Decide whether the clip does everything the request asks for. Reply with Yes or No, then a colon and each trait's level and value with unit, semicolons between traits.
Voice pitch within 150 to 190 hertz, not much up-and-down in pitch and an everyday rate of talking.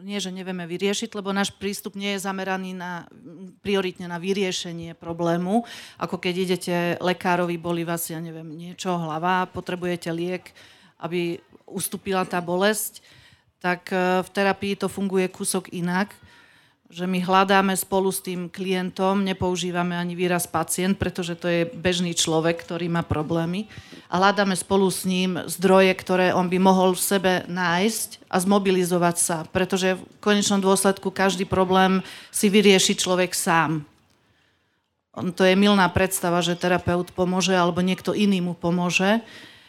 Yes: medium, 185 Hz; narrow, 1.7 semitones; average, 145 wpm